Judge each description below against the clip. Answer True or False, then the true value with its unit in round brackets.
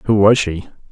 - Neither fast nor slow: True (195 wpm)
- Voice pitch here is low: True (100 Hz)